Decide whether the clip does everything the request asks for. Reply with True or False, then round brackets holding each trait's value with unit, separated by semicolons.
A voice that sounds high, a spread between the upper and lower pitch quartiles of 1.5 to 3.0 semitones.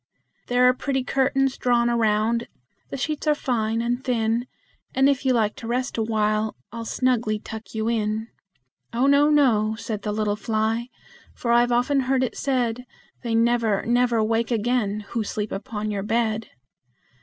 True (235 Hz; 2.5 semitones)